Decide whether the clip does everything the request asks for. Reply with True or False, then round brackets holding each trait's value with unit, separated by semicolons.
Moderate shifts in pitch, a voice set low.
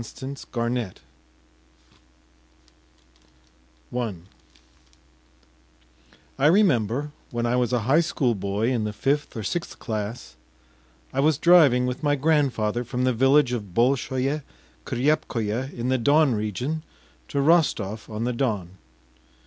True (4.1 semitones; 125 Hz)